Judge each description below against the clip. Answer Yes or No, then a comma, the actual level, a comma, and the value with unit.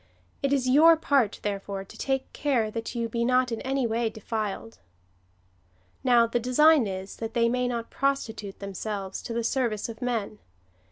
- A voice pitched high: Yes, high, 235 Hz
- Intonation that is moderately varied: Yes, average, 3.0 semitones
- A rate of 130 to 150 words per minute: No, average, 175 wpm